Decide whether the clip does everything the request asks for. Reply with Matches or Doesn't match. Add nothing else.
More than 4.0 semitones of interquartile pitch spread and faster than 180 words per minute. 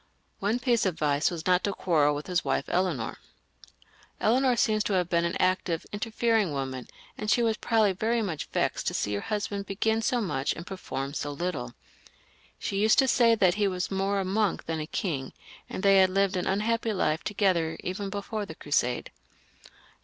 Matches